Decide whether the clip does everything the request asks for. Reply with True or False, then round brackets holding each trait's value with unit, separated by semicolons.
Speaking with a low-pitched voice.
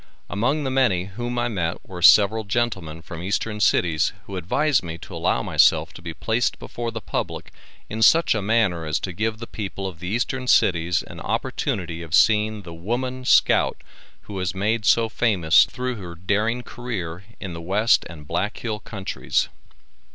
True (100 Hz)